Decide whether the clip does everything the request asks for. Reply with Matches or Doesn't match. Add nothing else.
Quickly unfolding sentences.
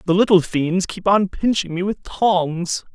Doesn't match